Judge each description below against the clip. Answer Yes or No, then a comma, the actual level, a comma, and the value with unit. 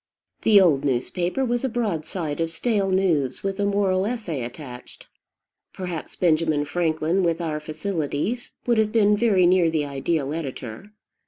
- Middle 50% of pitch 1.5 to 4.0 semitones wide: No, average, 4.9 semitones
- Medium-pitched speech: Yes, medium, 175 Hz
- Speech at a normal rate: Yes, average, 150 wpm